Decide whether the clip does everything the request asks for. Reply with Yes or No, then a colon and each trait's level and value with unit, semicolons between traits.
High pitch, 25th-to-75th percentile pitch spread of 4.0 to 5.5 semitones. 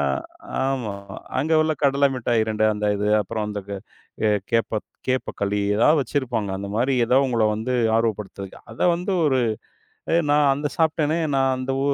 No: low, 120 Hz; average, 4.7 semitones